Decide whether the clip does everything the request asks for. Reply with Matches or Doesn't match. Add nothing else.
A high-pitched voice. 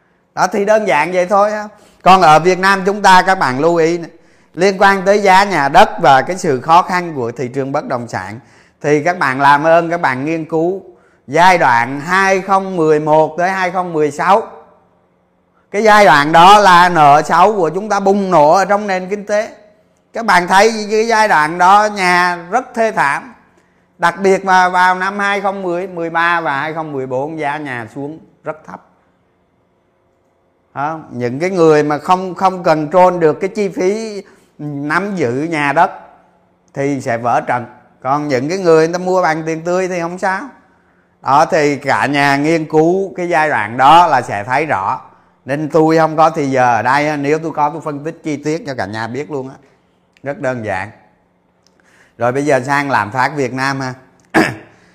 Doesn't match